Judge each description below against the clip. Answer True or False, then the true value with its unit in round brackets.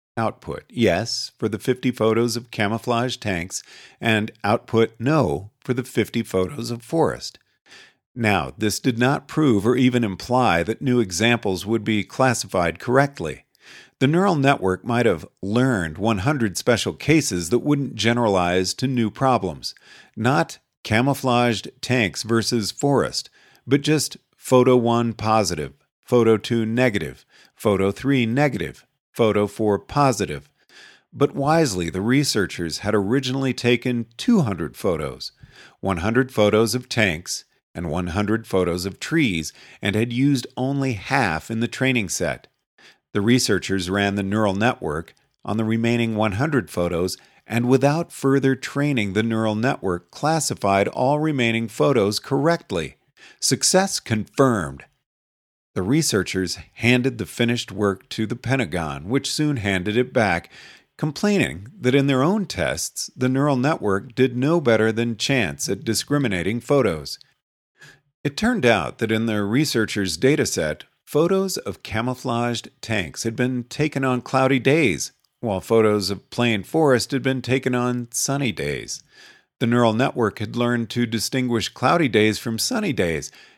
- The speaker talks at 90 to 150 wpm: True (135 wpm)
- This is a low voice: True (120 Hz)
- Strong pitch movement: False (4.0 semitones)